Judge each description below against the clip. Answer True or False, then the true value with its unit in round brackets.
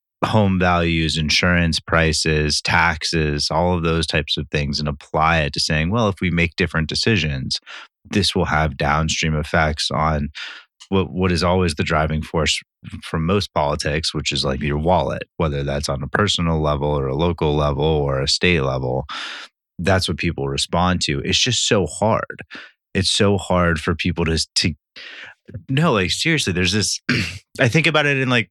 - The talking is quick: False (175 wpm)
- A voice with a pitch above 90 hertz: False (85 Hz)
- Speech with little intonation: False (3.5 semitones)